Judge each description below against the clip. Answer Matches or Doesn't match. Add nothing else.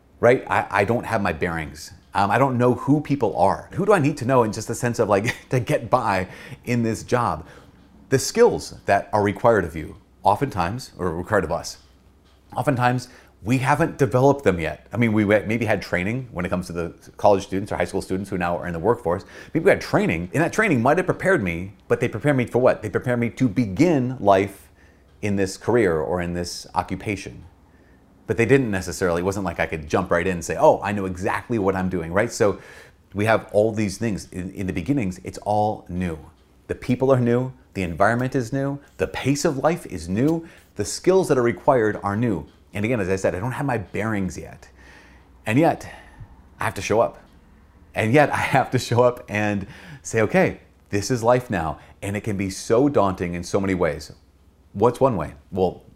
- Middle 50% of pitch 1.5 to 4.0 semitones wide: Doesn't match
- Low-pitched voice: Matches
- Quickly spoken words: Matches